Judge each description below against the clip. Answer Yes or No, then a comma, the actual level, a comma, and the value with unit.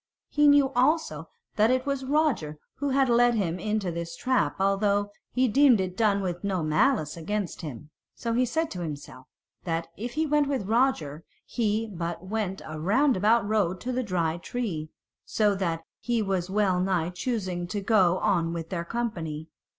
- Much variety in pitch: Yes, wide, 6.1 semitones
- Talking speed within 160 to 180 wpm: Yes, average, 175 wpm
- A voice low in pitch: No, high, 200 Hz